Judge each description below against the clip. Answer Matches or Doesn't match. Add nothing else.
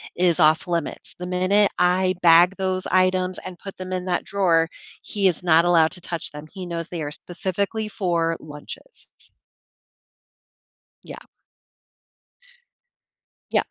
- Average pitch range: Doesn't match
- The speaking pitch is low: Doesn't match